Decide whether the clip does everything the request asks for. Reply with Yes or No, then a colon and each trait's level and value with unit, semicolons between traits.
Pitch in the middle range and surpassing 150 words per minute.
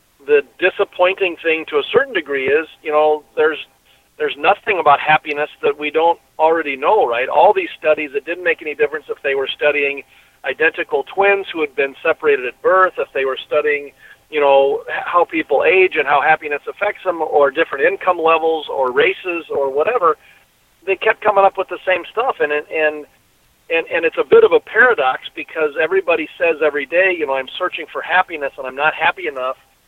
Yes: medium, 170 Hz; average, 195 wpm